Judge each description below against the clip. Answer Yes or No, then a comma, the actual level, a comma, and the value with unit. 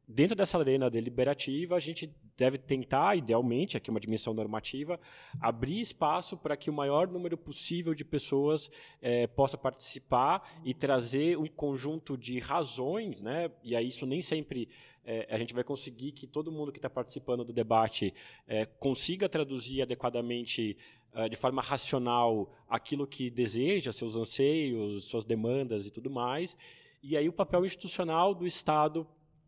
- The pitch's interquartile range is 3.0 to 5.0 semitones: Yes, average, 4.3 semitones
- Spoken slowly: No, average, 155 wpm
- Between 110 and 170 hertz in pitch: Yes, low, 135 Hz